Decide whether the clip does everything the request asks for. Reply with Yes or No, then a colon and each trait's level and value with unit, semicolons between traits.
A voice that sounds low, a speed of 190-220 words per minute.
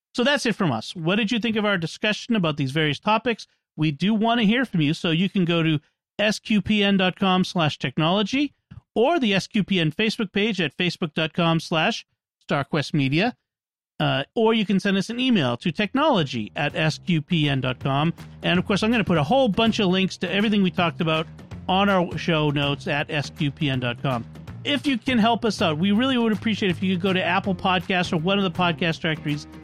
No: medium, 185 Hz; average, 200 wpm